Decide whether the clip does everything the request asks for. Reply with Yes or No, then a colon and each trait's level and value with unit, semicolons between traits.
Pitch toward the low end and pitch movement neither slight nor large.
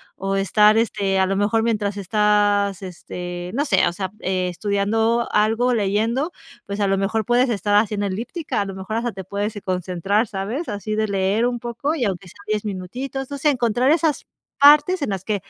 No: high, 210 Hz; average, 3.4 semitones